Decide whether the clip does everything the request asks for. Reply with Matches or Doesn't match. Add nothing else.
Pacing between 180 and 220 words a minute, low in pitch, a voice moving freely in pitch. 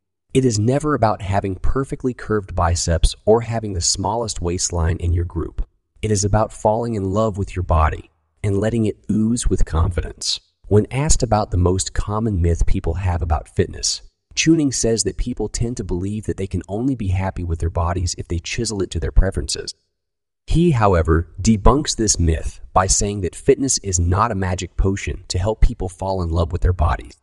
Doesn't match